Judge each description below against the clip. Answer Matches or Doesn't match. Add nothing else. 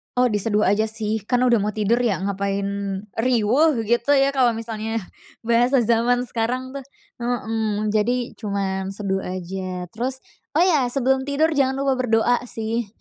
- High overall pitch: Matches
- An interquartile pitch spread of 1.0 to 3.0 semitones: Doesn't match